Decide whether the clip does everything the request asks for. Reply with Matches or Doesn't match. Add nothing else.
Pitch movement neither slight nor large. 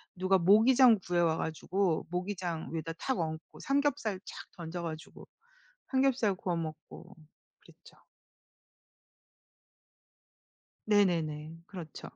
Matches